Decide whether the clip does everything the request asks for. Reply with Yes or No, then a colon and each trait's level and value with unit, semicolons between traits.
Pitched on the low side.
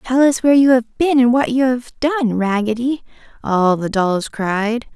No: high, 240 Hz